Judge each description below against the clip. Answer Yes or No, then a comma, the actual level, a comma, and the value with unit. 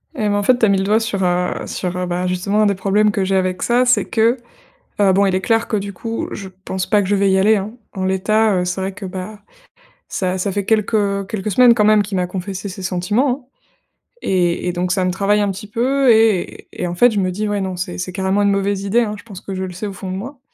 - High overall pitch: Yes, high, 200 Hz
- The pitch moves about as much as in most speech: No, narrow, 2.3 semitones